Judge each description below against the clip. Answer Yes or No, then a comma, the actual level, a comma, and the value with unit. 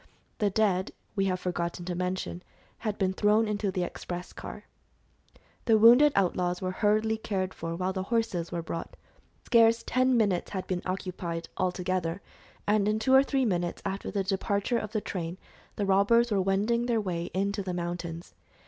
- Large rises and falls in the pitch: No, average, 3.2 semitones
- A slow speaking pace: No, average, 175 wpm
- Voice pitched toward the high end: Yes, high, 195 Hz